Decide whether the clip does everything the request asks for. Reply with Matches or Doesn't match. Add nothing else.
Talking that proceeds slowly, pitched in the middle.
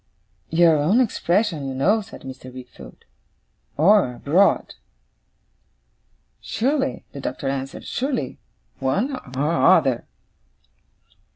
Matches